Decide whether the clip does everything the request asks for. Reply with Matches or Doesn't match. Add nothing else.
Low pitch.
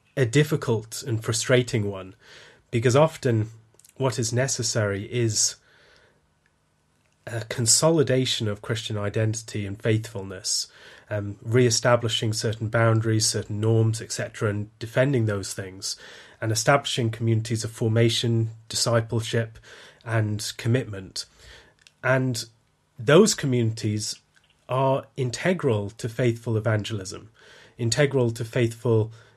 Matches